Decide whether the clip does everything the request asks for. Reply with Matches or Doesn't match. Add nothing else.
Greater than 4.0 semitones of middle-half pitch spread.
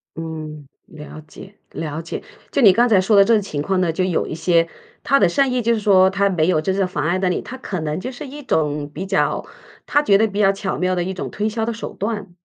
Matches